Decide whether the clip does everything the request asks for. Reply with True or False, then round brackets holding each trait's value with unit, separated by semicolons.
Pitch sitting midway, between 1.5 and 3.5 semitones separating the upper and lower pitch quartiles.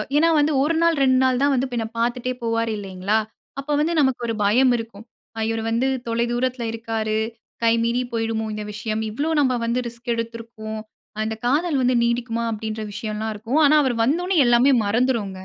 False (235 Hz; 2.8 semitones)